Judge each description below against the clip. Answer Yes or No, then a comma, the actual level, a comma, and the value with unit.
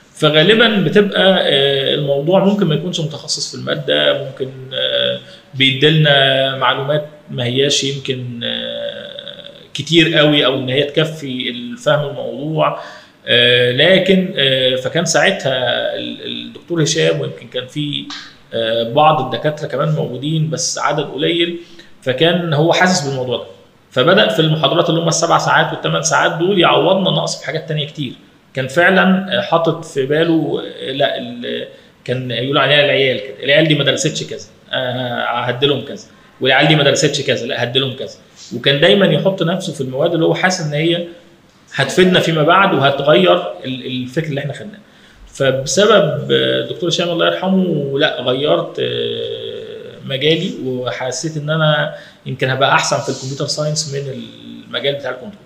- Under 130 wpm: No, fast, 135 wpm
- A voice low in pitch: No, medium, 150 Hz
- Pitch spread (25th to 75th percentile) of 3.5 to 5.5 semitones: Yes, average, 4.4 semitones